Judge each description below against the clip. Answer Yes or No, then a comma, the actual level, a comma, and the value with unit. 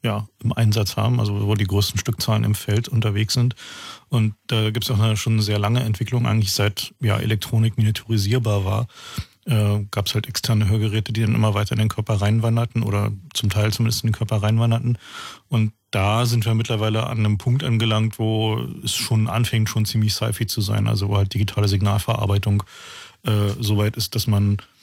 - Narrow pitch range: Yes, narrow, 1.6 semitones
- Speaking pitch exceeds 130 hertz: No, low, 110 Hz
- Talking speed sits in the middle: No, fast, 195 wpm